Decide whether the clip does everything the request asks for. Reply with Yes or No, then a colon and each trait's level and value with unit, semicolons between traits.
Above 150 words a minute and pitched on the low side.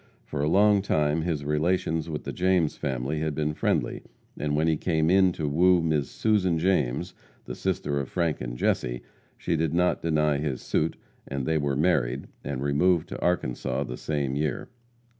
Yes: average, 180 wpm; very low, 75 Hz